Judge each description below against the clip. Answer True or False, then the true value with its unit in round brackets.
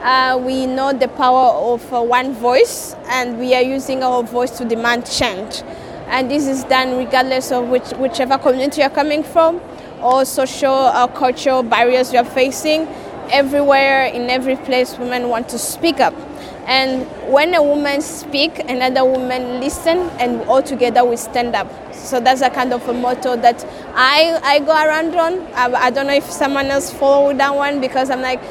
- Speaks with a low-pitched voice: False (260 Hz)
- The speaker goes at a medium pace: True (185 wpm)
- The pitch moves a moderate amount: False (2.0 semitones)